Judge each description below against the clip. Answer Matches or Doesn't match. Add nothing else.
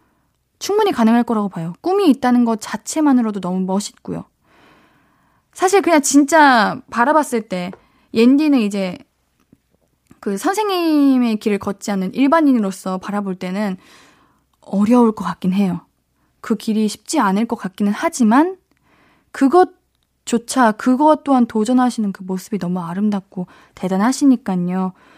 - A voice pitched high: Matches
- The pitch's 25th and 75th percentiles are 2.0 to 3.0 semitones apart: Doesn't match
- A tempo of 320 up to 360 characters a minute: Doesn't match